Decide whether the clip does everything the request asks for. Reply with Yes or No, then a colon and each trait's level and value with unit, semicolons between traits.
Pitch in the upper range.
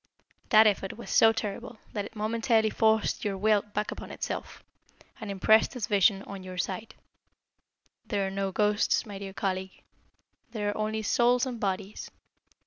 Yes: high, 210 Hz